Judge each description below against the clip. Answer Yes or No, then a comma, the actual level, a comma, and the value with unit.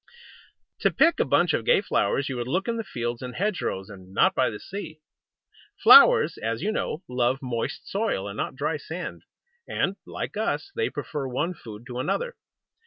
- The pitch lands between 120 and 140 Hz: Yes, low, 135 Hz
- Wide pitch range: Yes, wide, 8.4 semitones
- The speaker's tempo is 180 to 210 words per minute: Yes, average, 190 wpm